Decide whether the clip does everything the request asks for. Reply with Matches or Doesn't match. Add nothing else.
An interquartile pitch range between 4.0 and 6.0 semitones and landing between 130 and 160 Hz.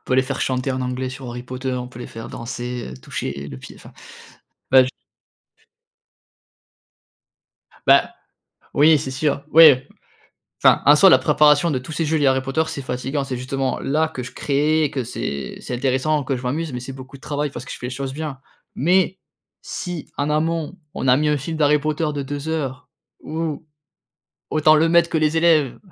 Doesn't match